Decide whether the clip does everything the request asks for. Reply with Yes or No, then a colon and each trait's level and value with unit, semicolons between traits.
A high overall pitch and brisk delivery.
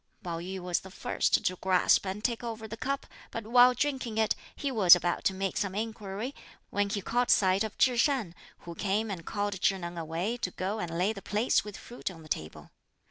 Yes: high, 200 Hz; fast, 220 wpm